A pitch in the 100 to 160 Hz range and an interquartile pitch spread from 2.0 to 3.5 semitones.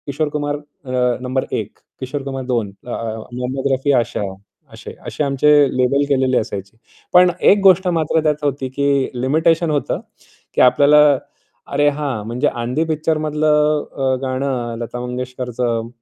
Yes: medium, 140 Hz; average, 3.0 semitones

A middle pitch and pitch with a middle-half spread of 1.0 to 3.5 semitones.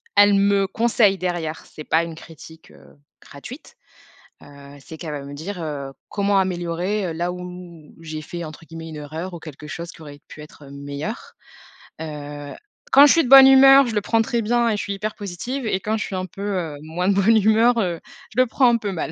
No: medium, 180 Hz; average, 5.2 semitones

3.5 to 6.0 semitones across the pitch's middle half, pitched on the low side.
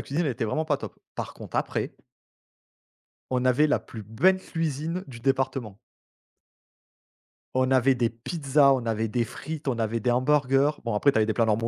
Yes: average, 4.0 semitones; low, 130 Hz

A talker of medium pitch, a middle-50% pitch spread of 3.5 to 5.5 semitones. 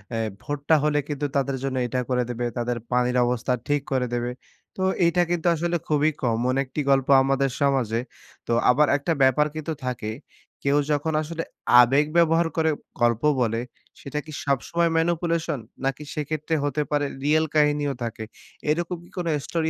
Yes: medium, 145 Hz; average, 3.9 semitones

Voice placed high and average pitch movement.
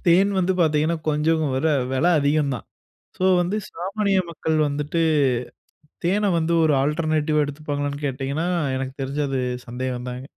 No: medium, 150 Hz; average, 3.2 semitones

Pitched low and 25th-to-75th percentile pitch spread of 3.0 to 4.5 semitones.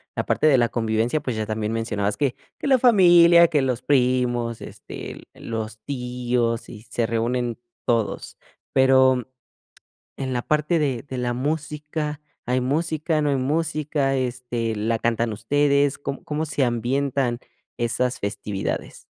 Yes: low, 125 Hz; average, 3.9 semitones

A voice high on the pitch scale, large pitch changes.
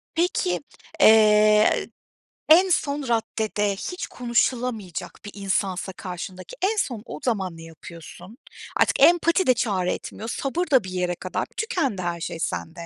Yes: high, 210 Hz; wide, 6.3 semitones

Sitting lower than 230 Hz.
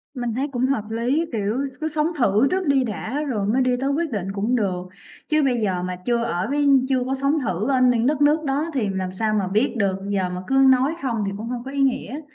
No: high, 245 Hz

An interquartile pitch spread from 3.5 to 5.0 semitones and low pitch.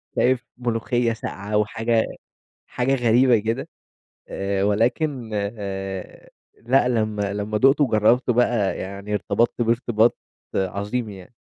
No: average, 3.1 semitones; low, 115 Hz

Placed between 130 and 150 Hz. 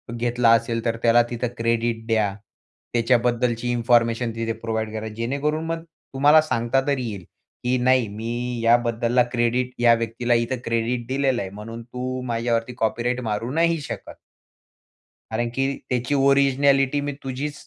No: low, 120 Hz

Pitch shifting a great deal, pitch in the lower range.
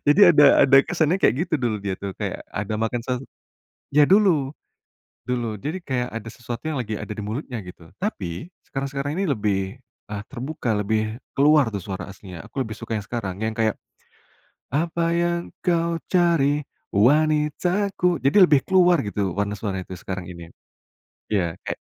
Yes: wide, 7.1 semitones; low, 125 Hz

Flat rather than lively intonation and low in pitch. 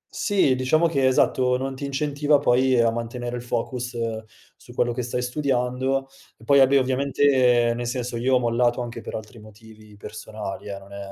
Yes: narrow, 2.3 semitones; low, 125 Hz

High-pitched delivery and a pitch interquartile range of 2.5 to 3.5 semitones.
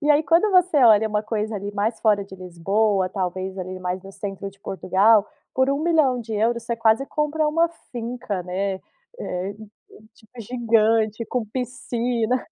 No: high, 220 Hz; average, 4.1 semitones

